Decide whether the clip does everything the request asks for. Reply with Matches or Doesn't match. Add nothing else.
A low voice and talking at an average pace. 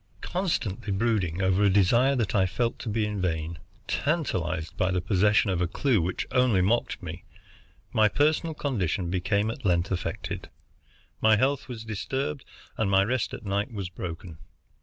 Matches